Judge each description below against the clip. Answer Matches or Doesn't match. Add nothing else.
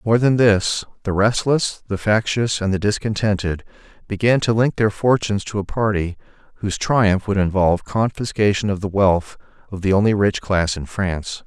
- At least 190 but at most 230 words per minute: Doesn't match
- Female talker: Doesn't match